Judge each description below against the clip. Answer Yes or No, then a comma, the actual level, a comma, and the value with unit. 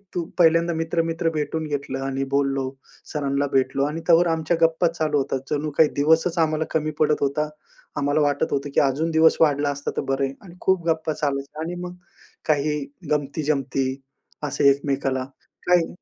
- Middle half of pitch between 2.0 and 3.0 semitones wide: Yes, narrow, 2.6 semitones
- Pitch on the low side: No, medium, 150 Hz